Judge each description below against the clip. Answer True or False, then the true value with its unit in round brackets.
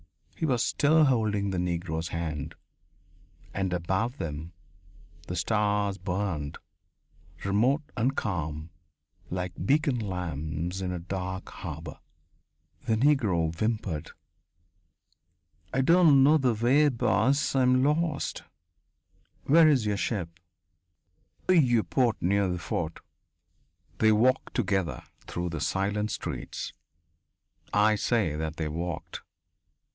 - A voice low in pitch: True (100 Hz)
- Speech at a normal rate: False (115 wpm)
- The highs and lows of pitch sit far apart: True (6.6 semitones)